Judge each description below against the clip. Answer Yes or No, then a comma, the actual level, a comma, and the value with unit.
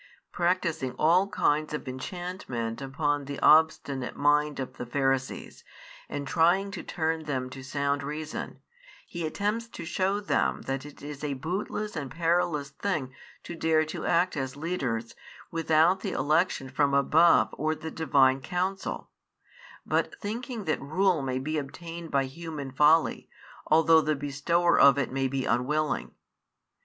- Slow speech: No, average, 150 wpm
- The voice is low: No, medium, 155 Hz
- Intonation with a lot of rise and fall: No, average, 3.8 semitones